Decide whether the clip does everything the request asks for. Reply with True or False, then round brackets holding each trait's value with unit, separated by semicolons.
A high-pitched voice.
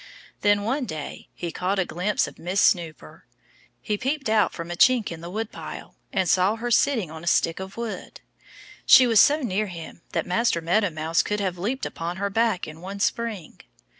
True (195 Hz)